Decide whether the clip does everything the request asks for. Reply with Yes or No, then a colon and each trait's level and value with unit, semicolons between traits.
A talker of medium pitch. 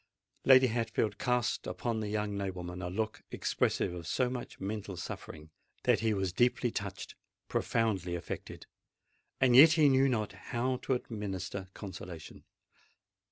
No: low, 105 Hz